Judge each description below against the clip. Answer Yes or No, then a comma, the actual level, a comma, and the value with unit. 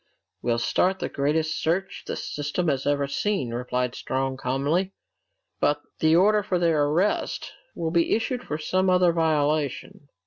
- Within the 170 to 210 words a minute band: No, average, 150 wpm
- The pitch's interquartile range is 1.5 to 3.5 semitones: No, average, 4.4 semitones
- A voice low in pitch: No, medium, 155 Hz